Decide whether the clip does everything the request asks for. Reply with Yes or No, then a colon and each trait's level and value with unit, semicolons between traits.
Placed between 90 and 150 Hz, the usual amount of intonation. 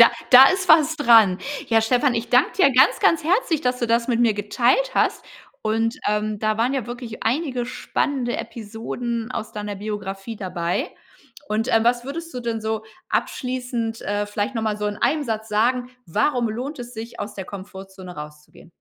No: high, 230 Hz; average, 3.1 semitones